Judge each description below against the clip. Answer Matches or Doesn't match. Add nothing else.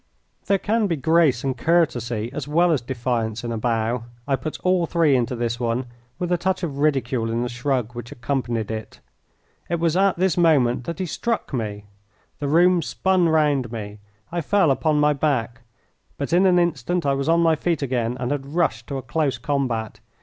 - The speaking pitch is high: Doesn't match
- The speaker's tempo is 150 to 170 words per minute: Doesn't match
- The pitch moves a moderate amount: Doesn't match